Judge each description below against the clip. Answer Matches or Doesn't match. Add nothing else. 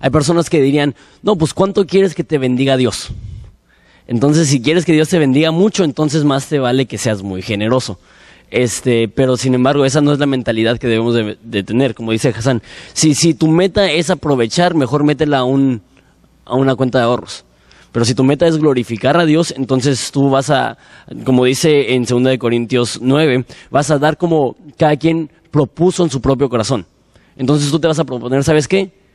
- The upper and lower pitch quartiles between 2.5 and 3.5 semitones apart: Doesn't match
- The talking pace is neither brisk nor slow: Doesn't match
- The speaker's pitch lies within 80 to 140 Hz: Matches